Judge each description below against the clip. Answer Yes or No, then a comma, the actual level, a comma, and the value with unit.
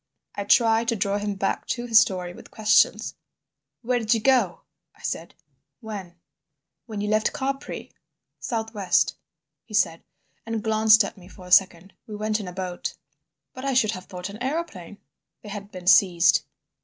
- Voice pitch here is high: Yes, high, 210 Hz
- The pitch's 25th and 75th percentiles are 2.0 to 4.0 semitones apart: Yes, average, 3.2 semitones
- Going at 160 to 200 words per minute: Yes, average, 175 wpm